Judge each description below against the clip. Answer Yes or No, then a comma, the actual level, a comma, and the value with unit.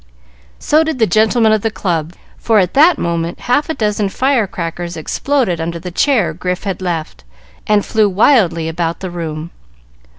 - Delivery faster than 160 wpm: Yes, average, 170 wpm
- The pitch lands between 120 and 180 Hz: No, high, 190 Hz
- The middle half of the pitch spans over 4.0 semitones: Yes, average, 4.9 semitones